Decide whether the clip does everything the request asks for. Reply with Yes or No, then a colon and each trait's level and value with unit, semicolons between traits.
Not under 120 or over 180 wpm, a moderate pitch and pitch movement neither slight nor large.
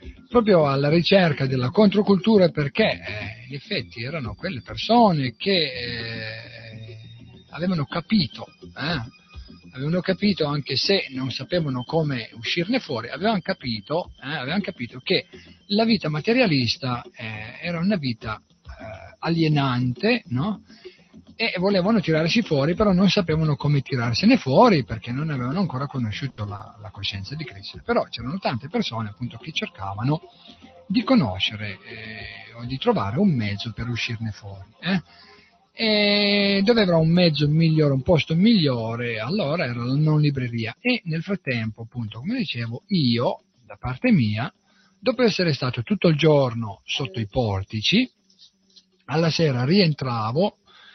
No: average, 140 wpm; medium, 145 Hz; wide, 8.5 semitones